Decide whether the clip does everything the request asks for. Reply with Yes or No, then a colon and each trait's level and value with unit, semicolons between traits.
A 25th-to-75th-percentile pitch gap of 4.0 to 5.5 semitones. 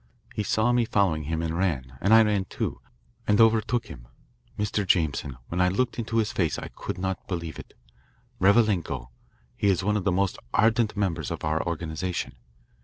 Yes: average, 4.5 semitones